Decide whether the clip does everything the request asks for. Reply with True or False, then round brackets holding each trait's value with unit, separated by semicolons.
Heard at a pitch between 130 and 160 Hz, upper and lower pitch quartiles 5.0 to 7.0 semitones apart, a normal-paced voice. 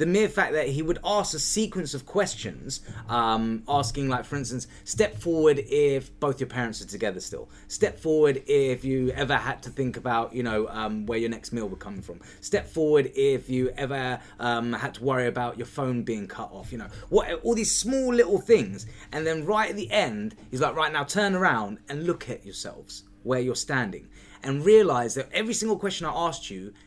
False (135 Hz; 5.6 semitones; 210 wpm)